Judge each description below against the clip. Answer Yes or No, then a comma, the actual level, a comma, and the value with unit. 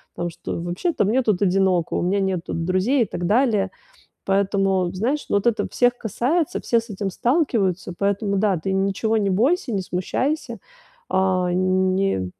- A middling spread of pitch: Yes, average, 3.6 semitones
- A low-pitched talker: No, high, 195 Hz